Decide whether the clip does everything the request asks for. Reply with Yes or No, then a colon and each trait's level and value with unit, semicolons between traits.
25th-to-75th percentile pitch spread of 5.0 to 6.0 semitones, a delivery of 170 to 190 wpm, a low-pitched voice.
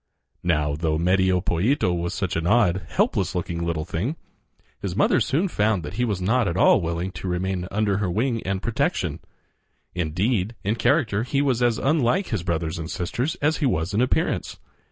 Yes: wide, 5.6 semitones; average, 185 wpm; very low, 95 Hz